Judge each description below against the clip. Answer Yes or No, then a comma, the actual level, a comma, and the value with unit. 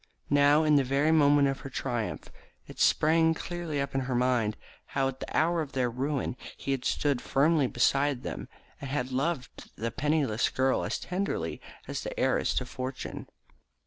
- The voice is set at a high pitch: No, medium, 140 Hz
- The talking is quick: No, average, 175 wpm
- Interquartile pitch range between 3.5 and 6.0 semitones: No, average, 2.8 semitones